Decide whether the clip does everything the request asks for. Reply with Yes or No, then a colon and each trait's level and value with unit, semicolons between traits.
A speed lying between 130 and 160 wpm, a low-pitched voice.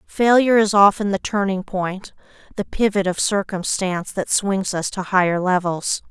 No: average, 155 wpm; high, 195 Hz